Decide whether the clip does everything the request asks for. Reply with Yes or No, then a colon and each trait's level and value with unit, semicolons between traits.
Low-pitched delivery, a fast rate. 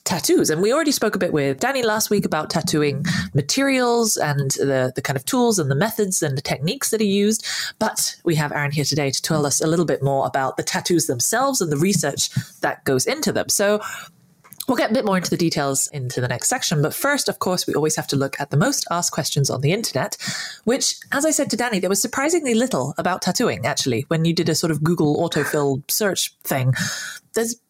No: medium, 170 Hz; fast, 230 wpm